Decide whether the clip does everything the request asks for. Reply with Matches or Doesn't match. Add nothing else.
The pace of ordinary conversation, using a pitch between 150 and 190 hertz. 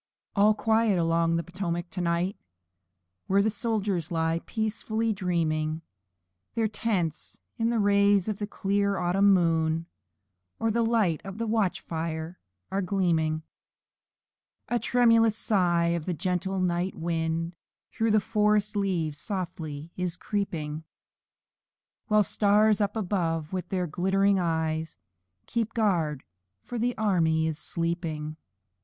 Doesn't match